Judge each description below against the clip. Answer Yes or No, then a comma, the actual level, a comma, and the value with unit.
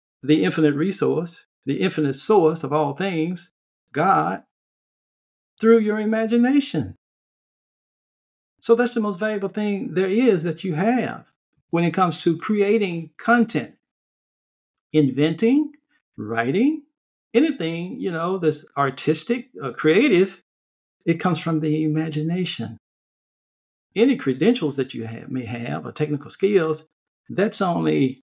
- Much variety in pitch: Yes, wide, 6.1 semitones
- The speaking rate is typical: No, slow, 120 wpm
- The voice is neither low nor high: Yes, medium, 170 Hz